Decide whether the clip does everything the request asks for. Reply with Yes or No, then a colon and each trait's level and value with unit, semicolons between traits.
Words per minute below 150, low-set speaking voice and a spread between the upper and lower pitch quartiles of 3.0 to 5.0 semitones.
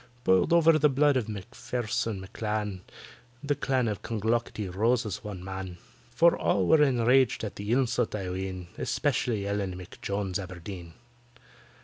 Yes: average, 140 wpm; low, 105 Hz; average, 4.7 semitones